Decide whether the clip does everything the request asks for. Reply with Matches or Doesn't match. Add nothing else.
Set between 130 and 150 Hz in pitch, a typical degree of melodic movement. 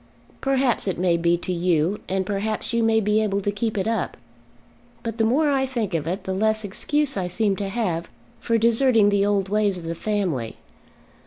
Doesn't match